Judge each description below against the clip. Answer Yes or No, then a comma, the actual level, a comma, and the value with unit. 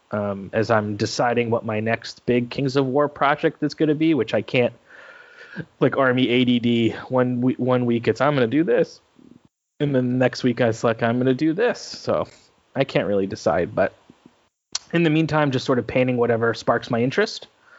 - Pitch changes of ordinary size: Yes, average, 3.5 semitones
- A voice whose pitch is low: Yes, low, 125 Hz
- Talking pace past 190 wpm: Yes, average, 200 wpm